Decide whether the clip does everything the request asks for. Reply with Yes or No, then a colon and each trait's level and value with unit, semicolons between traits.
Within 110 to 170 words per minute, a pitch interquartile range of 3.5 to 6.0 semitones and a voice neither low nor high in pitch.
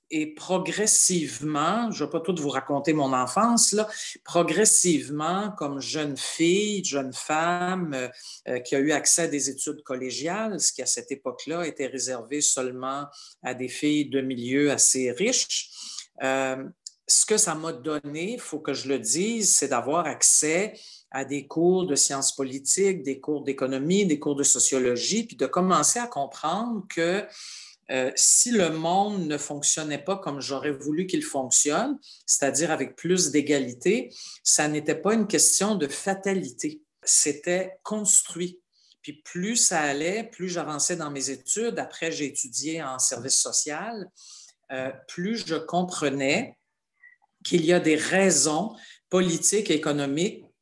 Yes: average, 155 wpm; average, 5.2 semitones; medium, 155 Hz